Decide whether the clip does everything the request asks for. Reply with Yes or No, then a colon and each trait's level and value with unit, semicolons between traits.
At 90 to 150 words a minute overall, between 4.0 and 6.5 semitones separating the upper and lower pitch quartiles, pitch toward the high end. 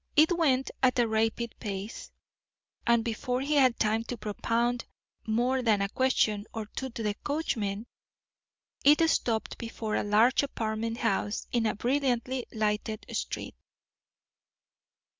No: slow, 135 wpm; average, 3.0 semitones; high, 230 Hz